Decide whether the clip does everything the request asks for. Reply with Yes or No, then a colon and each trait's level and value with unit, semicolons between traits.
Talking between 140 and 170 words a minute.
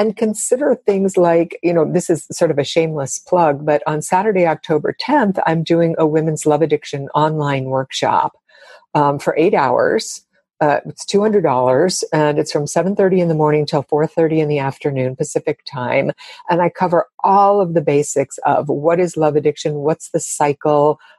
No: average, 185 wpm